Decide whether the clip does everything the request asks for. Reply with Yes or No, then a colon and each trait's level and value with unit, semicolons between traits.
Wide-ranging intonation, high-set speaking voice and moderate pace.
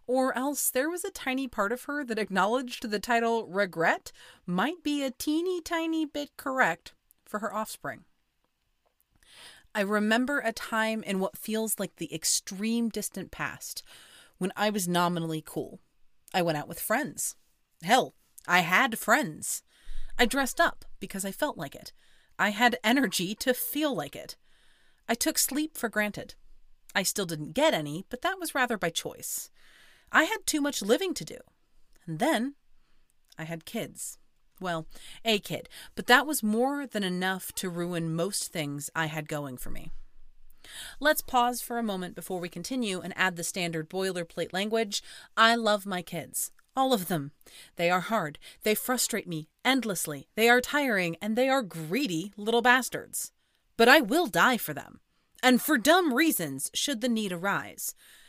Yes: wide, 6.2 semitones; high, 215 Hz; average, 165 wpm